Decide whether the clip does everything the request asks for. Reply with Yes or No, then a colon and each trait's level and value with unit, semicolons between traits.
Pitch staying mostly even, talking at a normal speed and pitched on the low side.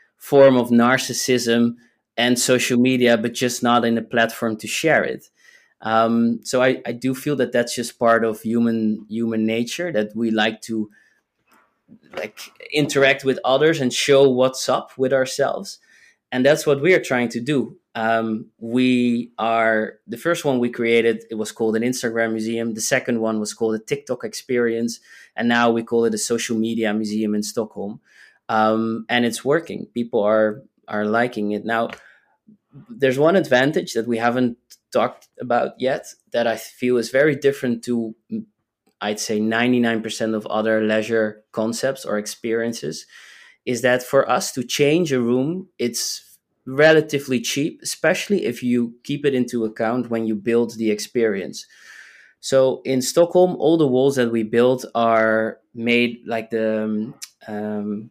Yes: narrow, 2.3 semitones; average, 160 wpm; low, 120 Hz